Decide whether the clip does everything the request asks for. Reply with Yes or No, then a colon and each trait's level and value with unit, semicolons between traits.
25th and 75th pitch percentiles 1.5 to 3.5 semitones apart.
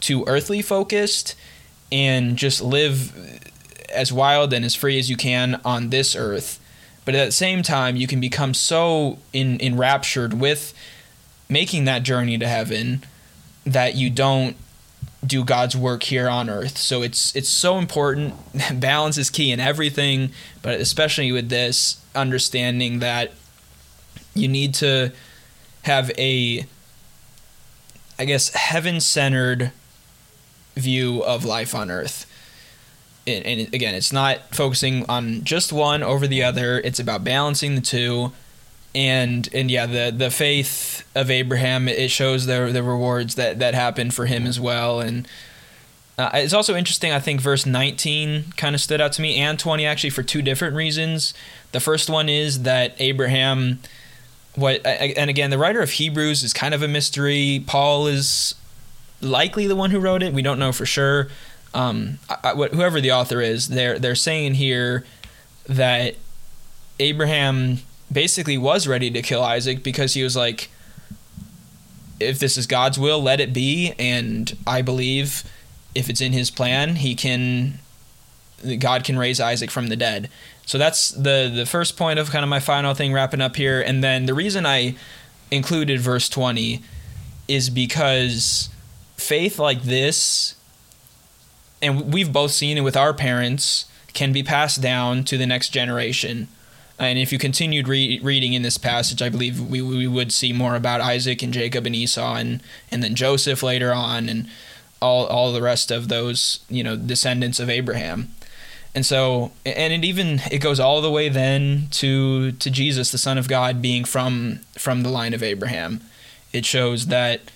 Yes: narrow, 2.4 semitones